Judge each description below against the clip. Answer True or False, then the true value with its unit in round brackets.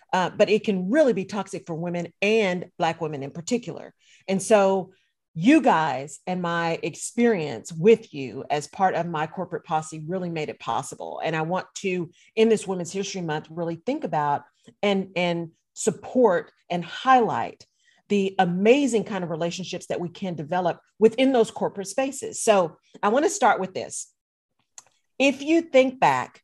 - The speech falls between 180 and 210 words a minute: False (170 wpm)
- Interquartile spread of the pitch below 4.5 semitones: False (4.9 semitones)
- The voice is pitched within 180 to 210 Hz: True (185 Hz)